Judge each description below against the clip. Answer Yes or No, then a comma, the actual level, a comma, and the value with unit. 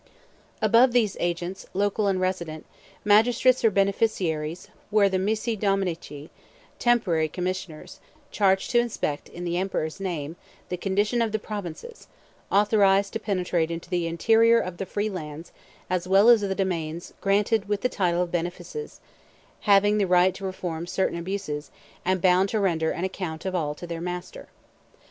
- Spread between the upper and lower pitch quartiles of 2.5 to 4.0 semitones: Yes, average, 3.1 semitones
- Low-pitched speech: No, high, 190 Hz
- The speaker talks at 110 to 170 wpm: Yes, average, 160 wpm